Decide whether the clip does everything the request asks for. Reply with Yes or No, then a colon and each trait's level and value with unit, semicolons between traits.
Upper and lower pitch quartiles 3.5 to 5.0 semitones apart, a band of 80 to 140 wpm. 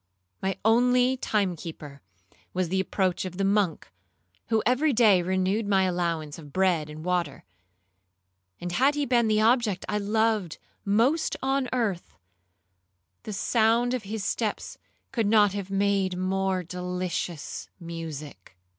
Yes: average, 3.9 semitones; slow, 135 wpm